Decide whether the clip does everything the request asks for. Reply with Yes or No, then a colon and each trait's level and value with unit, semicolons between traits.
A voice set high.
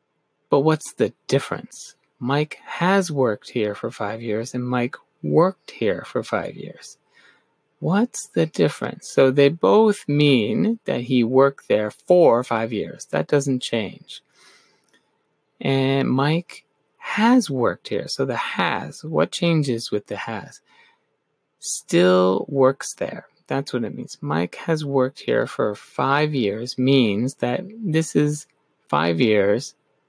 No: low, 135 Hz